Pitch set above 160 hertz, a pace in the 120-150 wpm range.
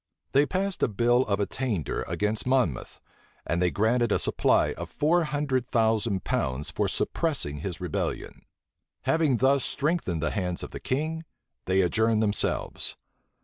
No: low, 115 Hz; average, 145 wpm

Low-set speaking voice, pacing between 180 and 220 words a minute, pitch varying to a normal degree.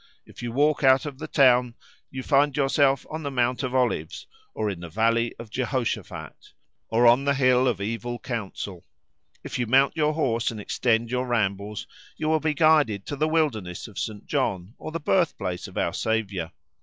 Yes: low, 125 Hz; average, 190 wpm; average, 4.4 semitones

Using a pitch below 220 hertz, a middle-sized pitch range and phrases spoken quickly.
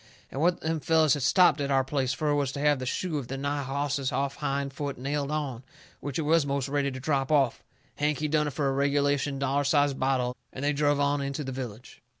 No: medium, 140 Hz; narrow, 1.5 semitones; fast, 240 wpm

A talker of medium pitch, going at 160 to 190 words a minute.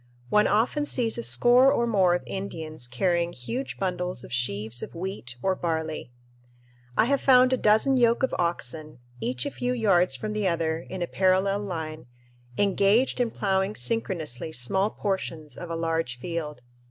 Yes: medium, 180 Hz; average, 165 wpm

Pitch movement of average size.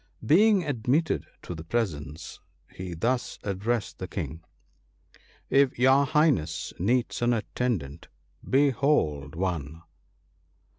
No: wide, 8.7 semitones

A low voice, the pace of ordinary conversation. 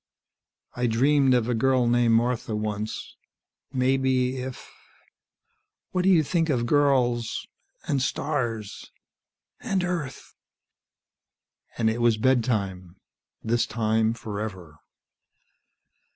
No: low, 120 Hz; slow, 105 wpm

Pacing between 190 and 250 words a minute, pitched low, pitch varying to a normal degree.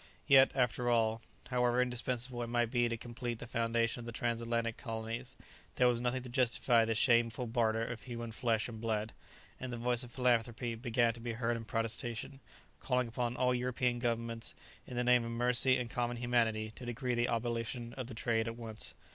No: average, 195 wpm; low, 120 Hz; narrow, 1.2 semitones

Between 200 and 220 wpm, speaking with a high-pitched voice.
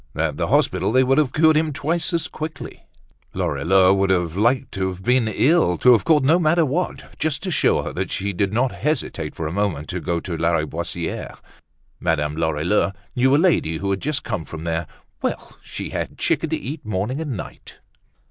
No: fast, 205 wpm; low, 105 Hz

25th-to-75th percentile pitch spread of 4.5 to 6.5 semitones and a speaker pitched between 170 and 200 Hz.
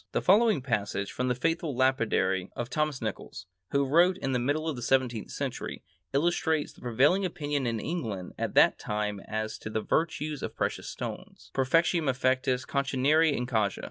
No: average, 4.9 semitones; low, 130 Hz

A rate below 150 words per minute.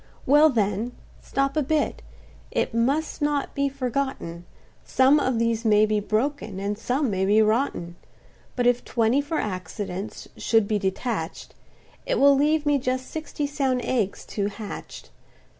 Yes: average, 140 wpm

